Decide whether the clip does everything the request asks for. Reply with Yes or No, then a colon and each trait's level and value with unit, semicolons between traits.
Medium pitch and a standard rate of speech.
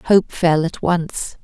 Yes: medium, 170 Hz; average, 165 wpm